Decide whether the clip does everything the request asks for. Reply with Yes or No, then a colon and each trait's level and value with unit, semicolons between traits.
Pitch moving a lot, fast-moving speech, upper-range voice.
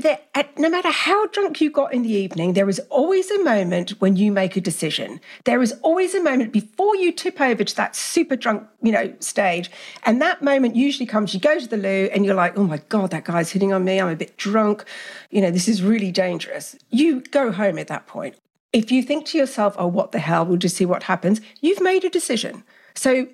Yes: wide, 7.3 semitones; fast, 235 wpm; high, 220 Hz